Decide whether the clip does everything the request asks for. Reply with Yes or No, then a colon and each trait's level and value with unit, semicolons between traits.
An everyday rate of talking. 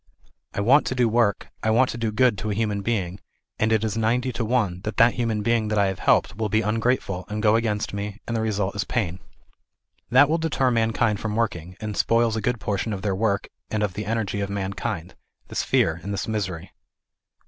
No: fast, 225 wpm